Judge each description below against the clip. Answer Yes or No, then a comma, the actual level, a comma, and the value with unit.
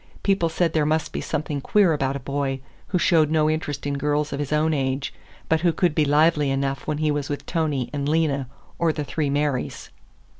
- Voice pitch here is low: No, medium, 150 Hz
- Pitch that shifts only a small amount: Yes, narrow, 2.1 semitones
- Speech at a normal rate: No, fast, 215 wpm